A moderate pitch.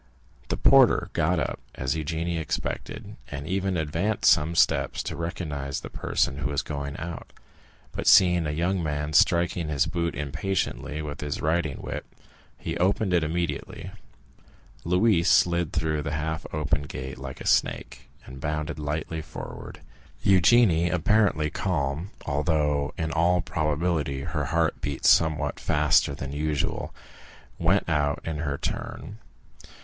No: very low, 80 Hz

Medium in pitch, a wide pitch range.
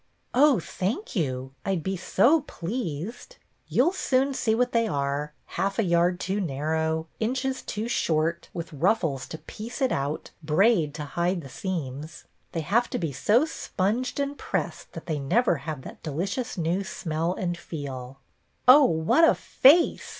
Yes: medium, 180 Hz; wide, 7.2 semitones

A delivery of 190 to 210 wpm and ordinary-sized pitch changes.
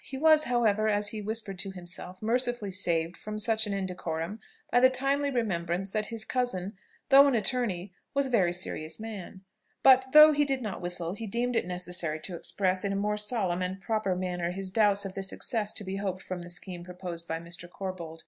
Yes: fast, 205 wpm; average, 4.2 semitones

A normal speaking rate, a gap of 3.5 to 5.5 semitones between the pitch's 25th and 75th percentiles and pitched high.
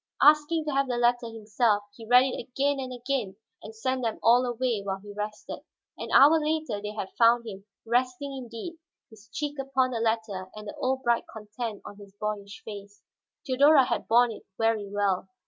Yes: average, 190 wpm; average, 3.8 semitones; high, 235 Hz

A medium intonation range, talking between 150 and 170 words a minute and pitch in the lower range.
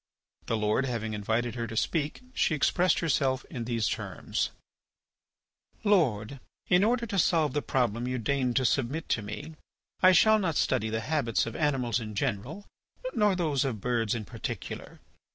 No: wide, 5.9 semitones; average, 165 wpm; low, 130 Hz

